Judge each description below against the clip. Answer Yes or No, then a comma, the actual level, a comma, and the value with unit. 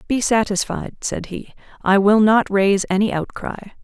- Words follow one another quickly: No, average, 155 wpm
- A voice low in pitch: No, high, 205 Hz